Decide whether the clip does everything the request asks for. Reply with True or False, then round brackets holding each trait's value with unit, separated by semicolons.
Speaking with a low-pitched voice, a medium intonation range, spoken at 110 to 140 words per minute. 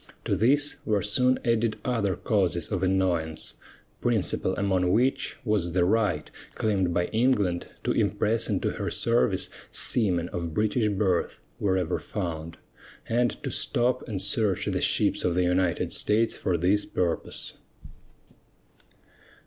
True (100 Hz; 4.0 semitones; 135 wpm)